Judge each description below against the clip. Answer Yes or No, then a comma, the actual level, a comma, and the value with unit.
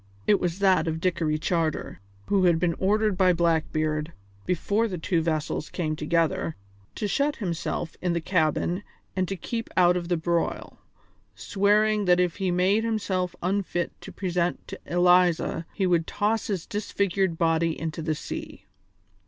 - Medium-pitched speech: Yes, medium, 180 Hz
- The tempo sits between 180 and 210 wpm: No, average, 160 wpm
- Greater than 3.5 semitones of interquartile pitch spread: No, average, 2.9 semitones